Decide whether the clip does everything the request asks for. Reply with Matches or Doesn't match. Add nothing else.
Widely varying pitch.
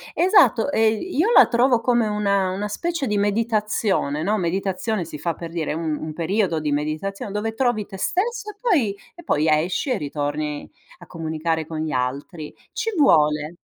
Matches